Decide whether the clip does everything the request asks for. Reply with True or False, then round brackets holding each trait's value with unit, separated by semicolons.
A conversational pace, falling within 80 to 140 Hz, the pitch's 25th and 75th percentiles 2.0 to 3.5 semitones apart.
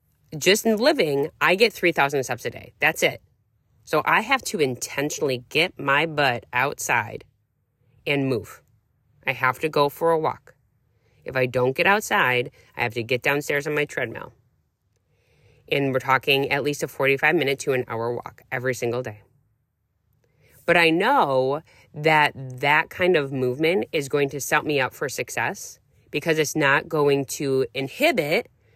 True (165 wpm; 135 Hz; 3.1 semitones)